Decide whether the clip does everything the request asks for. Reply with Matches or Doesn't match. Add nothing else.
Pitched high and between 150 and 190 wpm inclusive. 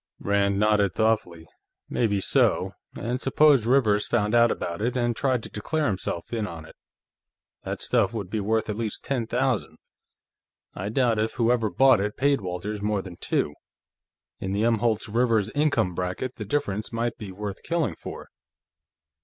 Doesn't match